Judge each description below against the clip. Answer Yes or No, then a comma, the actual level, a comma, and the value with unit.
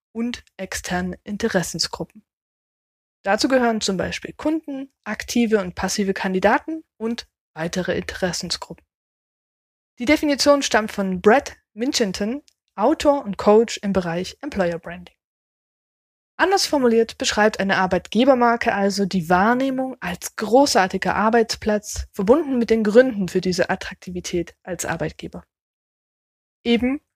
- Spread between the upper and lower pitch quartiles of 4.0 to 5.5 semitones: Yes, average, 4.9 semitones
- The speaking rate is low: Yes, slow, 110 wpm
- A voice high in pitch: Yes, high, 215 Hz